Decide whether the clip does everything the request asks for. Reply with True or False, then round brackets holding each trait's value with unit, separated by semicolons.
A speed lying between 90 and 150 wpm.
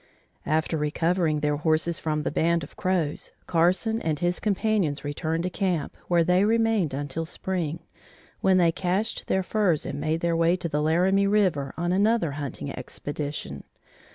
False (160 wpm)